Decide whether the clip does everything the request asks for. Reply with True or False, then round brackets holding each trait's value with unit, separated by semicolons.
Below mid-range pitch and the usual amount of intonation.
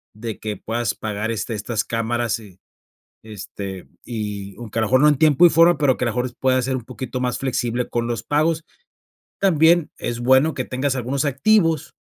True (125 Hz; 4.2 semitones)